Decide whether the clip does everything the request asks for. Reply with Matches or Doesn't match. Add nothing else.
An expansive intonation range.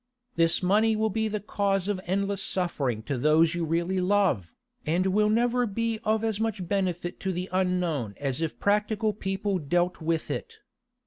Doesn't match